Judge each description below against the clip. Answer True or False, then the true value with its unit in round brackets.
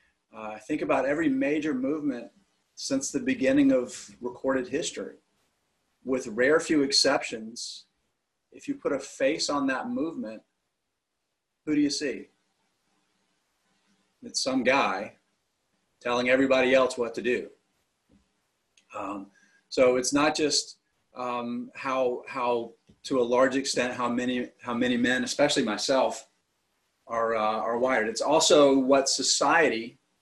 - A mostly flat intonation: False (3.8 semitones)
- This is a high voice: False (135 Hz)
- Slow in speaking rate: True (130 wpm)